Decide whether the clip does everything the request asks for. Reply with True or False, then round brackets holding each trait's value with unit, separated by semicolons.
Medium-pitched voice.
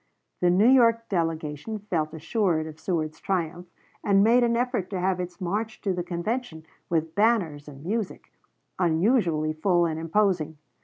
True (180 Hz)